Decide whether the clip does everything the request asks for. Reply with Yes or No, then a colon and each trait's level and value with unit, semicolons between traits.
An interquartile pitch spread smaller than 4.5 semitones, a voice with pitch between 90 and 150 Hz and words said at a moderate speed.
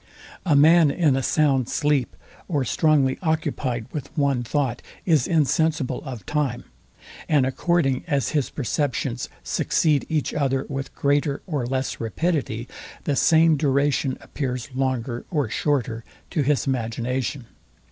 No: average, 2.9 semitones; medium, 140 Hz; slow, 130 wpm